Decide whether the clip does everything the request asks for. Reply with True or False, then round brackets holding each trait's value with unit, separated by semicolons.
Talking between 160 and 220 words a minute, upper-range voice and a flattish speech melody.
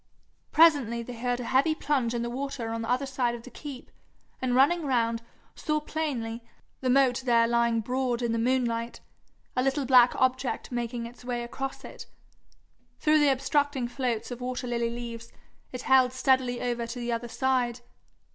True (175 wpm; 250 Hz; 2.0 semitones)